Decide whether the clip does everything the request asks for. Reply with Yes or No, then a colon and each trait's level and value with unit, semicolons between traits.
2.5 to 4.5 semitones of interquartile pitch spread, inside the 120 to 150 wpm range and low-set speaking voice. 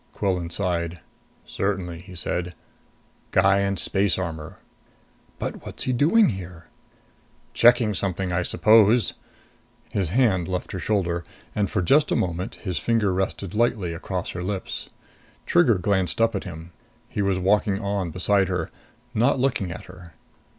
Yes: average, 2.8 semitones; average, 145 wpm; very low, 95 Hz